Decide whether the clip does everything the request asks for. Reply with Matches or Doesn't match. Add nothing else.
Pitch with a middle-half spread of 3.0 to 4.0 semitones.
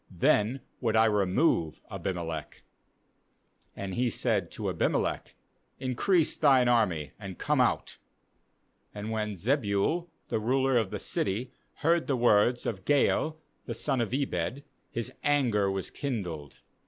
Doesn't match